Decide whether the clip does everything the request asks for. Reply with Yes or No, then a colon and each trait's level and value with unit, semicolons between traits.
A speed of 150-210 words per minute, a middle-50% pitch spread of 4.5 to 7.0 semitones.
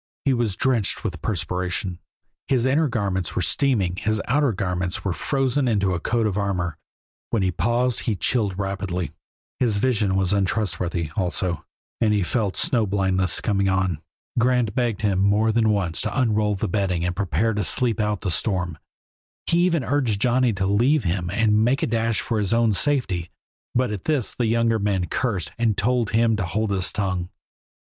No: average, 180 wpm; average, 3.9 semitones